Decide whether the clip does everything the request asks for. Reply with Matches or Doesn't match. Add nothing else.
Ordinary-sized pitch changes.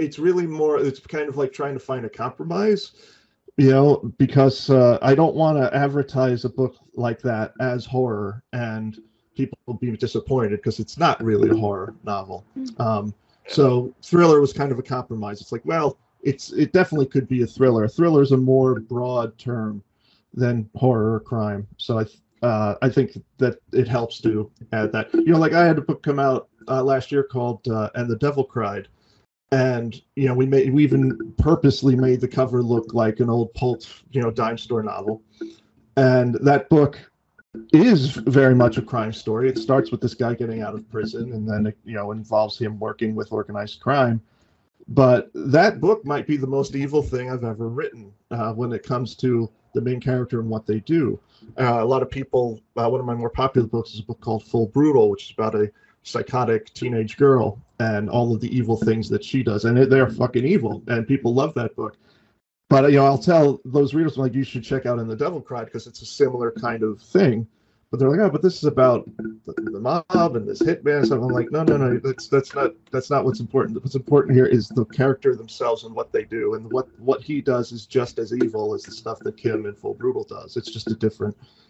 Matches